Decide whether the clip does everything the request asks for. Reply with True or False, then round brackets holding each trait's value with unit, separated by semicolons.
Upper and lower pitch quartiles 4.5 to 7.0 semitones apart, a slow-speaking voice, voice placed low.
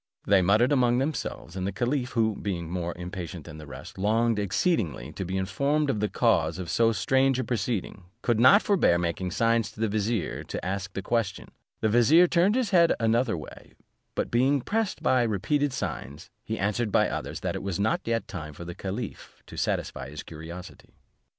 False (5.5 semitones; 195 wpm; 110 Hz)